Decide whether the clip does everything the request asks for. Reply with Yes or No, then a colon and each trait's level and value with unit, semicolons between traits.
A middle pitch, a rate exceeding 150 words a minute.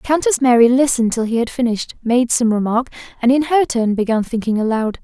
No: high, 240 Hz; fast, 205 wpm